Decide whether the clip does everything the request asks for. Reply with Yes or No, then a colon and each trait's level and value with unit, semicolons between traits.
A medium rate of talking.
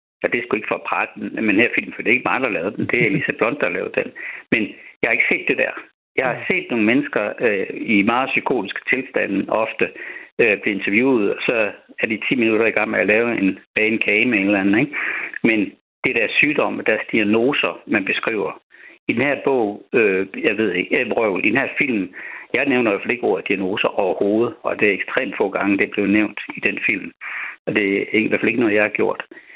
No: fast, 250 wpm